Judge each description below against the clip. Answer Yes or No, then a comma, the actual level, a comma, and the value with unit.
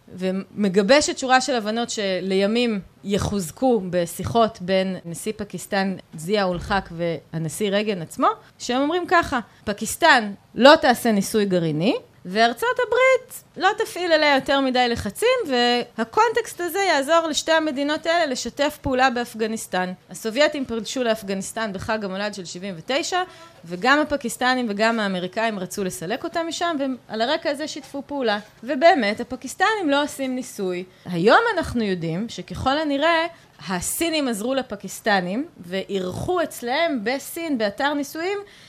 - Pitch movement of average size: No, wide, 7.2 semitones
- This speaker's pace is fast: No, average, 120 wpm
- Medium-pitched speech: No, high, 240 Hz